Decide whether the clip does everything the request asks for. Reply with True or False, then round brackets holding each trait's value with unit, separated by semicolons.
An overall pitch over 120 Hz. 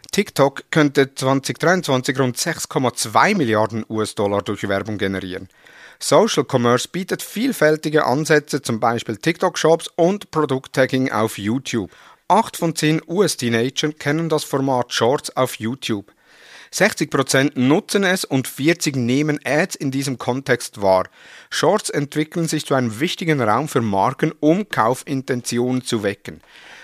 True (135 Hz)